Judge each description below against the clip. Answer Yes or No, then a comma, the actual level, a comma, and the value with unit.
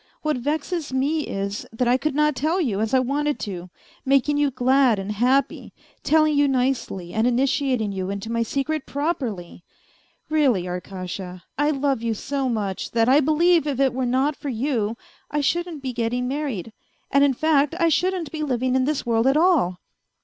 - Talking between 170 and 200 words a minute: Yes, average, 185 wpm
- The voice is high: Yes, very high, 265 Hz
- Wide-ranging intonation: No, average, 4.6 semitones